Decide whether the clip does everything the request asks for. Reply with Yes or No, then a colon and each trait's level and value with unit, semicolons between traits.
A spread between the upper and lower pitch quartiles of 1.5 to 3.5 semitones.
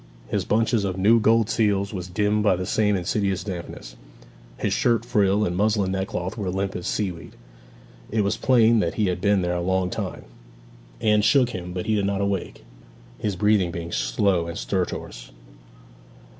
Yes: average, 2.8 semitones